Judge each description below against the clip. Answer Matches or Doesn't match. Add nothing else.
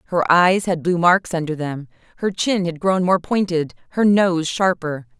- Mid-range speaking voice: Matches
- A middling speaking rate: Matches